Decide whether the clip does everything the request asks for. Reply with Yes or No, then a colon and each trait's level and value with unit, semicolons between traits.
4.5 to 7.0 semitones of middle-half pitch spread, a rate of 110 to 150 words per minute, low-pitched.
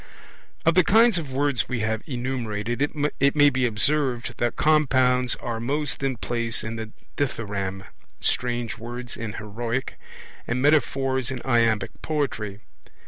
No: average, 3.5 semitones; average, 140 wpm; low, 125 Hz